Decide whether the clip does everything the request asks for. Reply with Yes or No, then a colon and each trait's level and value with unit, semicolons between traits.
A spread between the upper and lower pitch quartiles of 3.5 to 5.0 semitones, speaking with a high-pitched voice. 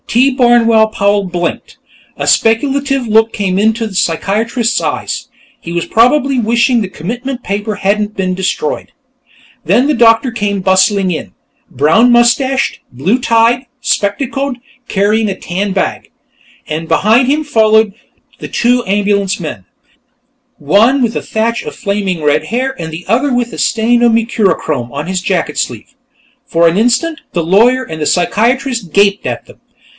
Yes: average, 4.4 semitones; high, 220 Hz